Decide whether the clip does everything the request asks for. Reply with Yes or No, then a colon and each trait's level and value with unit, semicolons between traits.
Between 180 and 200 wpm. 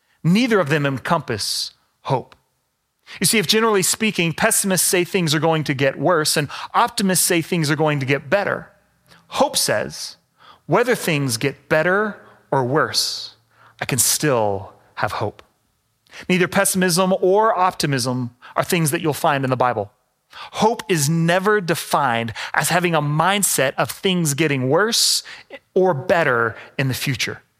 No: average, 150 wpm